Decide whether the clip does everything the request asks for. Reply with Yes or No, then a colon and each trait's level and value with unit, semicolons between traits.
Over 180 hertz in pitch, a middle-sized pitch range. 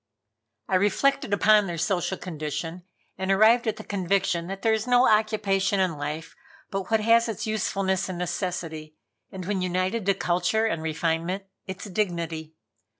Yes: high, 190 Hz; average, 3.5 semitones